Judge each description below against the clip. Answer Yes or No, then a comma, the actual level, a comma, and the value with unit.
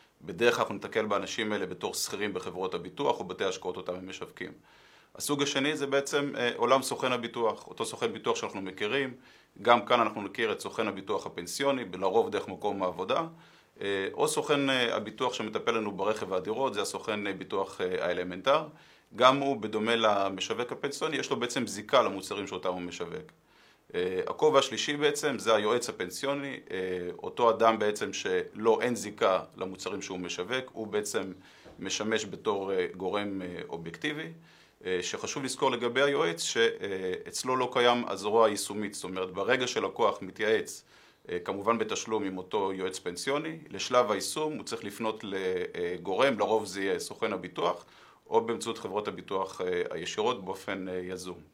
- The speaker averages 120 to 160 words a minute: Yes, average, 140 wpm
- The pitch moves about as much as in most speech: No, wide, 7.8 semitones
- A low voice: Yes, low, 120 Hz